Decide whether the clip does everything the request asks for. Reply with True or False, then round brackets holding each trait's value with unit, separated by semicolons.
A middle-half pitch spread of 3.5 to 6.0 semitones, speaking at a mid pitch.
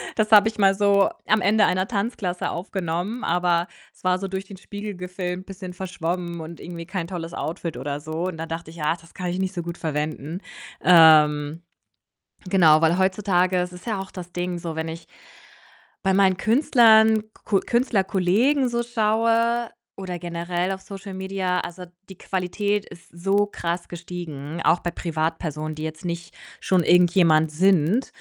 False (2.8 semitones; 180 Hz)